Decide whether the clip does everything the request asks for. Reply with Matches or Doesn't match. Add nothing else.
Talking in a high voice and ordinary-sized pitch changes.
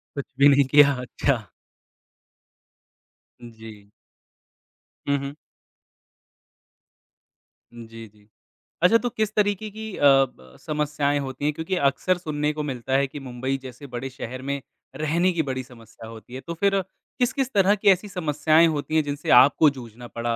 Doesn't match